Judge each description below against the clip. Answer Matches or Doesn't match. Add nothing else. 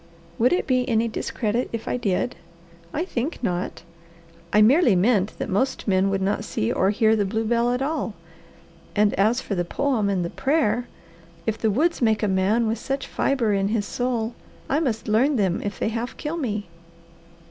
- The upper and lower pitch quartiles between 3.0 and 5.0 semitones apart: Matches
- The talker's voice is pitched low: Doesn't match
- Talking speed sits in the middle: Matches